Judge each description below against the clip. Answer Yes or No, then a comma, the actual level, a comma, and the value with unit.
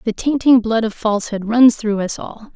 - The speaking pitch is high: Yes, high, 225 Hz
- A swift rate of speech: Yes, fast, 210 wpm